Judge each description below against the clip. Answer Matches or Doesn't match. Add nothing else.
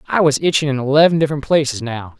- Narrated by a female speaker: Doesn't match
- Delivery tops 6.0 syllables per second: Matches